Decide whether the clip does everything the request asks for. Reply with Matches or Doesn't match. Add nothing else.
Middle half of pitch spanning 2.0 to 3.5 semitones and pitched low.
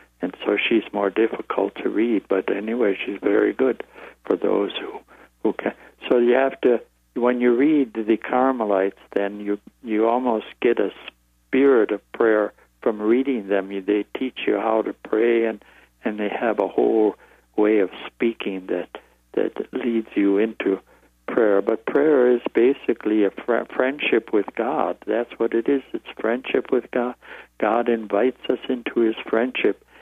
Matches